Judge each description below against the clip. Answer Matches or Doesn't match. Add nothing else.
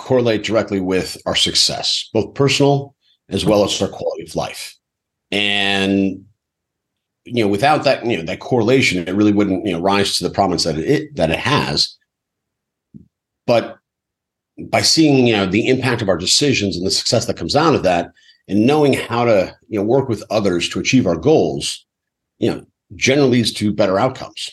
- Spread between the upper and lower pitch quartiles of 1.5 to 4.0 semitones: Doesn't match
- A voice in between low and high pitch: Doesn't match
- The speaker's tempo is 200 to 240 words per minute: Doesn't match